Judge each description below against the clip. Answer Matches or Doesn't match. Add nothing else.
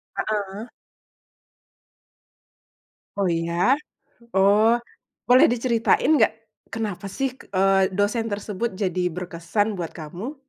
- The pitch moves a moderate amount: Matches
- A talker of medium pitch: Doesn't match